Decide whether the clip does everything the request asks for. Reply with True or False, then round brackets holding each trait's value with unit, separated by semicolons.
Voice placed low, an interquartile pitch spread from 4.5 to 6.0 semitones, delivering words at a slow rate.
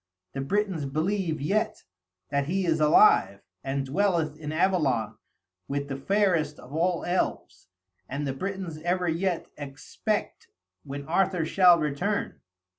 False (160 Hz; 4.8 semitones; 130 wpm)